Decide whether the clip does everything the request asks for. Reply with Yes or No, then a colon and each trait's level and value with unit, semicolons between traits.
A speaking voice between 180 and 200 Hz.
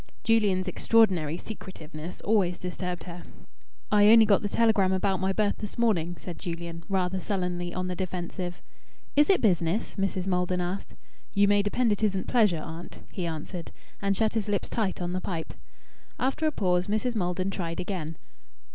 Yes: medium, 185 Hz